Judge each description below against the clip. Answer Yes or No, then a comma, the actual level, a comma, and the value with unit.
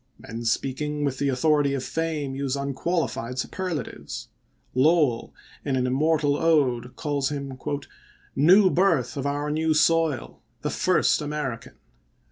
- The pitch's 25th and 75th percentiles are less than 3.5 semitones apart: Yes, average, 3.1 semitones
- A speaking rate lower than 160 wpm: Yes, average, 140 wpm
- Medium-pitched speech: Yes, medium, 145 Hz